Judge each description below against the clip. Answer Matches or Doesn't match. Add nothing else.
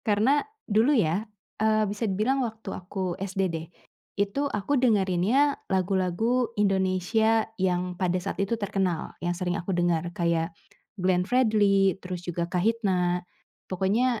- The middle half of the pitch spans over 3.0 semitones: Matches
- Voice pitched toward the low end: Doesn't match